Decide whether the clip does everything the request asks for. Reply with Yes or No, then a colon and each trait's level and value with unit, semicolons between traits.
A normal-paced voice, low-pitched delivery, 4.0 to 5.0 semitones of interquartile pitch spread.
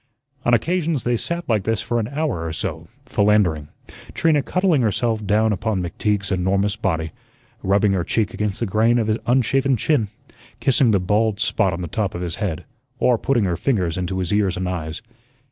Yes: average, 190 wpm; low, 105 Hz; average, 4.4 semitones